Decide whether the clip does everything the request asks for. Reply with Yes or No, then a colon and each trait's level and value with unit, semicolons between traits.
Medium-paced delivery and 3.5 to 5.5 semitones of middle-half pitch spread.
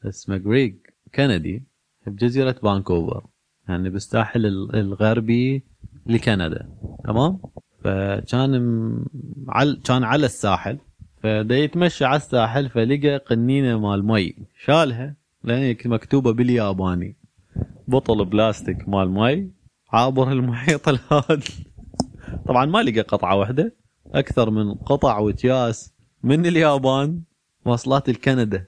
Yes: average, 100 wpm; average, 4.7 semitones